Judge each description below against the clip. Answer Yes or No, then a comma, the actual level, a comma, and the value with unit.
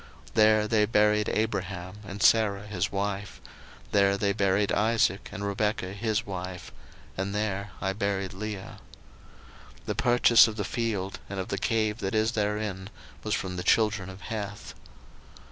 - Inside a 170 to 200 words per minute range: No, average, 160 wpm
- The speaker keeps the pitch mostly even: Yes, narrow, 1.9 semitones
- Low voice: Yes, low, 100 Hz